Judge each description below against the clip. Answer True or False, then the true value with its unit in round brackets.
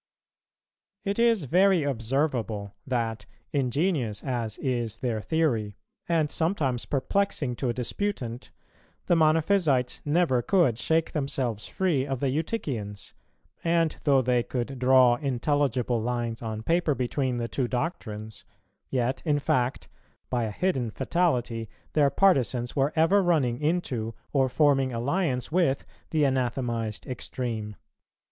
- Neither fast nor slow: False (125 wpm)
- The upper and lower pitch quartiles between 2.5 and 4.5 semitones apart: False (4.9 semitones)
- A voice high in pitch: False (130 Hz)